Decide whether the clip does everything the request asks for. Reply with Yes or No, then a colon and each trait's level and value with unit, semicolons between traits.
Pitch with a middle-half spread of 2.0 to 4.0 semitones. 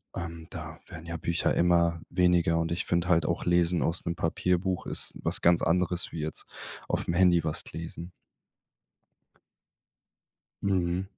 No: narrow, 1.2 semitones